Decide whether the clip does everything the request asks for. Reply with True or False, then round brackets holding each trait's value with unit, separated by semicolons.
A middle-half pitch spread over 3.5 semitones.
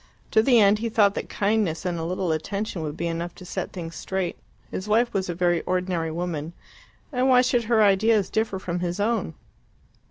True (4.1 semitones)